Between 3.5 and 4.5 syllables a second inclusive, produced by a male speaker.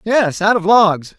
Yes: 3.7 syllables/s; male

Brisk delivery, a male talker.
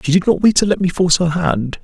Yes: fast, 325 wpm; male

